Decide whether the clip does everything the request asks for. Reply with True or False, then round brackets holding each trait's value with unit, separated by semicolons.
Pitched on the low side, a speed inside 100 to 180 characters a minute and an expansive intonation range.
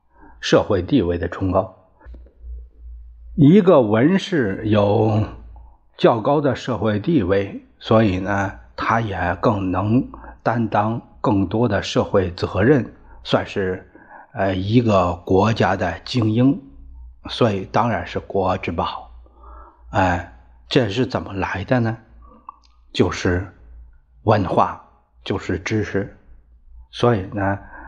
True (95 Hz; 155 characters per minute; 7.8 semitones)